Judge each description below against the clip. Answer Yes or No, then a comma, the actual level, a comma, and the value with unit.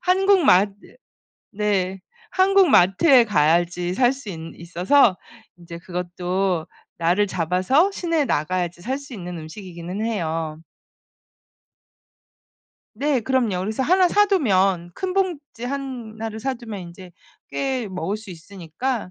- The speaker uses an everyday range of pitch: No, wide, 7.1 semitones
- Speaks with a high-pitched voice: Yes, high, 200 Hz